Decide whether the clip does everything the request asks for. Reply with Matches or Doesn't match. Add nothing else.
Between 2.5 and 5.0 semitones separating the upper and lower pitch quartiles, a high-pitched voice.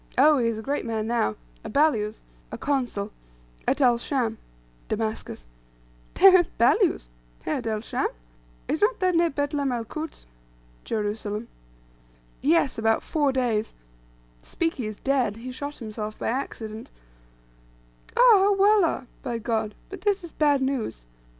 Doesn't match